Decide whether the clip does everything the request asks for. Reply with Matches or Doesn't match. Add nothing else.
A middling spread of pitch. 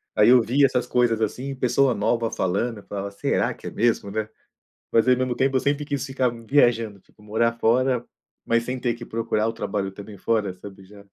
Matches